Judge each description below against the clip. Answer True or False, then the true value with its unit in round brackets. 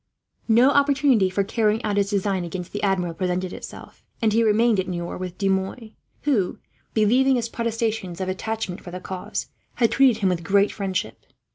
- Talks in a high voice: True (205 Hz)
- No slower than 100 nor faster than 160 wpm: False (180 wpm)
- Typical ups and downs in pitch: True (3.5 semitones)